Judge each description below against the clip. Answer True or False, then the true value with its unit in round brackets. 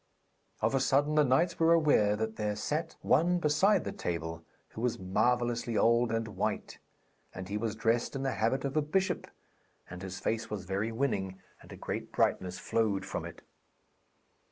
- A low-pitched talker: True (115 Hz)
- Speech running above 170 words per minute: True (180 wpm)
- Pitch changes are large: True (5.8 semitones)